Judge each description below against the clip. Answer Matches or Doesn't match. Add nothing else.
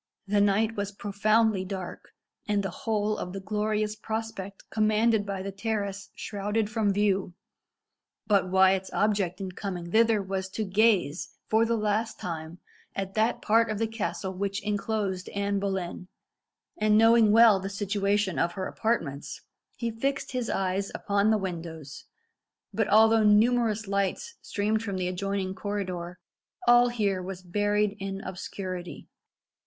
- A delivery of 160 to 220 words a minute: Doesn't match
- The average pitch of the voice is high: Matches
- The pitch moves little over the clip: Matches